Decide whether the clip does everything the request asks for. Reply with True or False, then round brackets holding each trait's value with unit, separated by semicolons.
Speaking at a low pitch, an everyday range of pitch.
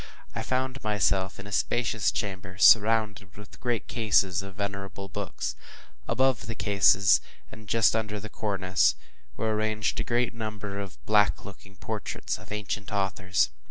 False (105 Hz; 2.1 semitones)